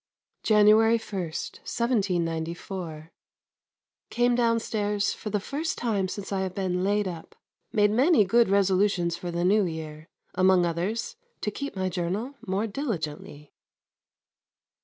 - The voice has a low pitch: No, high, 195 Hz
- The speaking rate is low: Yes, slow, 125 wpm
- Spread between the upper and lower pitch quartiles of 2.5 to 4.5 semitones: Yes, average, 3.9 semitones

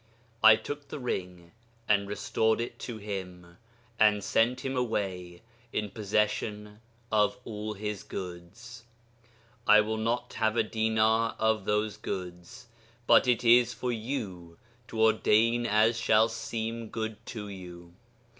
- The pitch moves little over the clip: Yes, narrow, 2.2 semitones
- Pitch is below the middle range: Yes, low, 110 Hz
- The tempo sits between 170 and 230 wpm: No, slow, 135 wpm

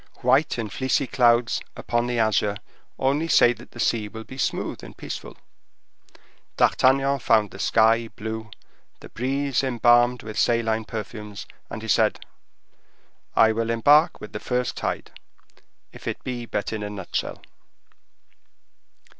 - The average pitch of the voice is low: Yes, low, 115 Hz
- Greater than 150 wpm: No, average, 140 wpm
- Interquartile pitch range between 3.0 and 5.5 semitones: No, narrow, 2.5 semitones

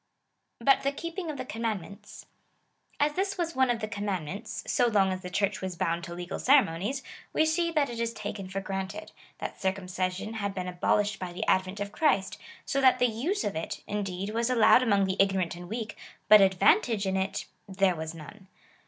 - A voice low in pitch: No, high, 205 Hz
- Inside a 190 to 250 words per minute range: Yes, average, 200 wpm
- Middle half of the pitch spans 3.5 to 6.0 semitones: Yes, average, 4.4 semitones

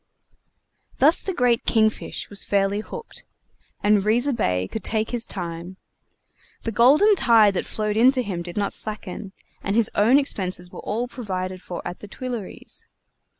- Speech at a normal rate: Yes, average, 165 wpm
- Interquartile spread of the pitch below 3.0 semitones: No, average, 4.1 semitones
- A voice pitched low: No, high, 215 Hz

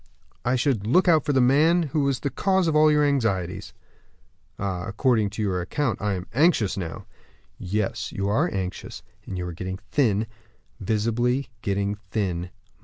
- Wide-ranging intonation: Yes, wide, 6.5 semitones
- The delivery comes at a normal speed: Yes, average, 170 wpm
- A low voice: Yes, low, 110 Hz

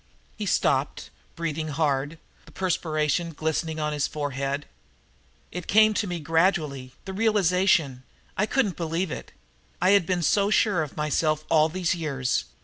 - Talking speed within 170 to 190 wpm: No, average, 145 wpm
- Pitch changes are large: No, average, 3.7 semitones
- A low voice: No, medium, 160 Hz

